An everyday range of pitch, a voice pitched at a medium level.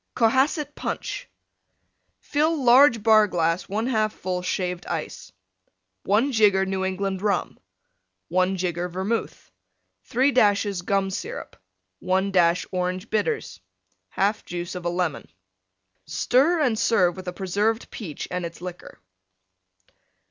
No: average, 4.0 semitones; high, 195 Hz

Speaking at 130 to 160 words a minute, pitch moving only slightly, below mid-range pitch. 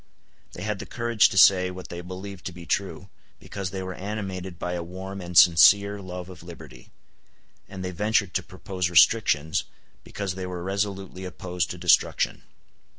No: average, 170 wpm; narrow, 1.8 semitones; very low, 95 Hz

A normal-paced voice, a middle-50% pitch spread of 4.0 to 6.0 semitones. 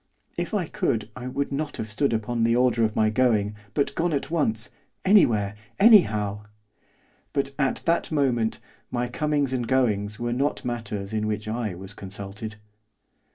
Yes: average, 160 wpm; average, 4.6 semitones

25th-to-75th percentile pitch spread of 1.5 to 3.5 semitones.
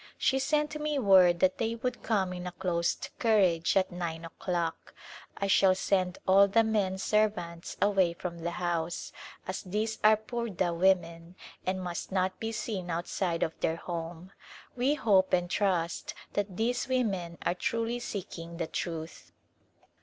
No: average, 4.0 semitones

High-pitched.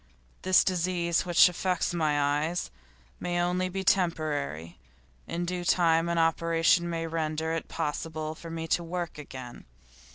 No: medium, 165 Hz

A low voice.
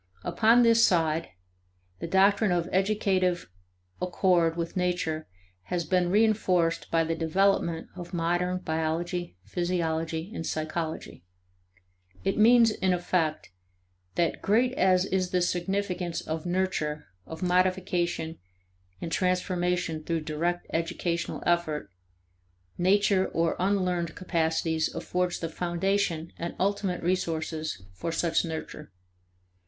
No: medium, 175 Hz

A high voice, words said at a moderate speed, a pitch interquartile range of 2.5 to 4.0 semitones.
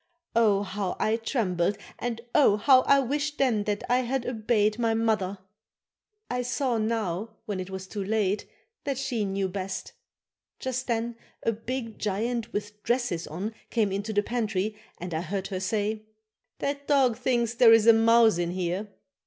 Yes: high, 220 Hz; average, 170 wpm; average, 3.1 semitones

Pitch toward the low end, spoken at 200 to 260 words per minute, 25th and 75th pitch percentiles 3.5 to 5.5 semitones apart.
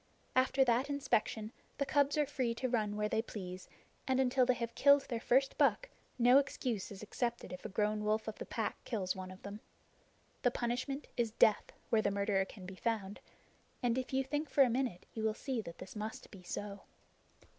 No: high, 230 Hz; fast, 205 wpm; average, 4.0 semitones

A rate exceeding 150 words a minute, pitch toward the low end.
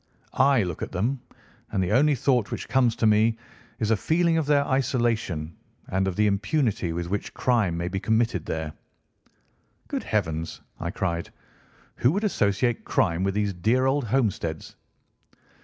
Yes: average, 160 wpm; low, 105 Hz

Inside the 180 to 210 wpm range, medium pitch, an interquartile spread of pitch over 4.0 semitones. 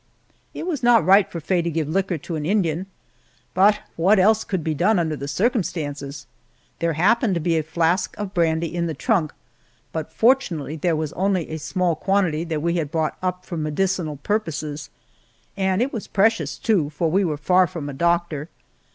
No: average, 190 wpm; medium, 170 Hz; average, 3.7 semitones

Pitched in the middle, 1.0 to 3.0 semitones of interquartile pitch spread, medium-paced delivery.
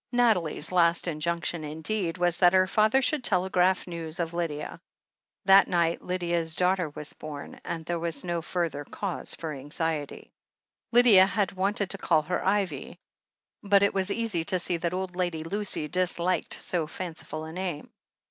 Yes: medium, 175 Hz; narrow, 2.6 semitones; average, 160 wpm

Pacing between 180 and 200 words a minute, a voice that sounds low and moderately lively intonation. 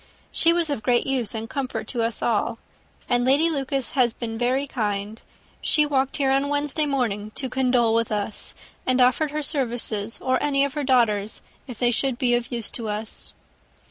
No: average, 190 wpm; very high, 250 Hz; average, 3.3 semitones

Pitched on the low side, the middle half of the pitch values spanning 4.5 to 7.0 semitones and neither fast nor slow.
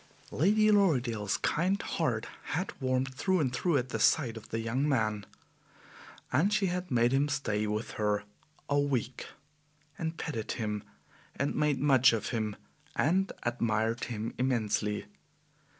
Yes: low, 130 Hz; wide, 5.4 semitones; average, 145 wpm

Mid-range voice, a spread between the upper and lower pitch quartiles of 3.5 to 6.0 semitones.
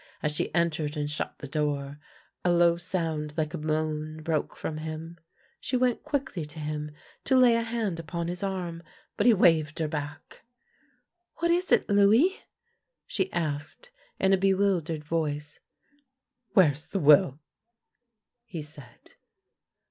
Yes: medium, 165 Hz; average, 5.0 semitones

